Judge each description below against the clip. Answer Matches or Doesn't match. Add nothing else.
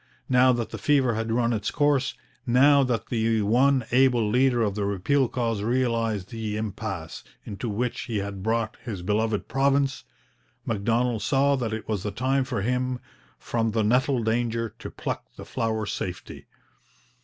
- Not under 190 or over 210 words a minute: Doesn't match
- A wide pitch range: Doesn't match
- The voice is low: Matches